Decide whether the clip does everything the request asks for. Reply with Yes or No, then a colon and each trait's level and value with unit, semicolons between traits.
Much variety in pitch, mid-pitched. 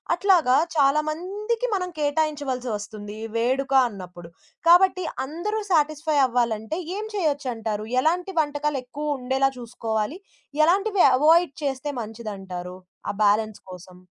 No: wide, 6.8 semitones; very high, 280 Hz